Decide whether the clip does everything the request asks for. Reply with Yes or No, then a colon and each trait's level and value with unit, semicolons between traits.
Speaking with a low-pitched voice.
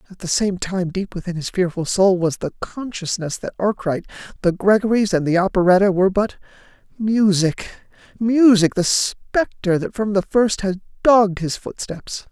No: high, 195 Hz